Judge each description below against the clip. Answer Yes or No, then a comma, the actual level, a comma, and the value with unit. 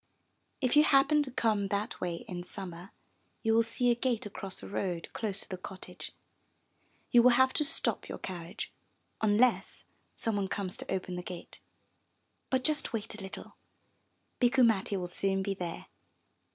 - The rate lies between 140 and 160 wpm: No, average, 170 wpm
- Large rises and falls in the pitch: No, average, 4.5 semitones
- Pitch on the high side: Yes, high, 205 Hz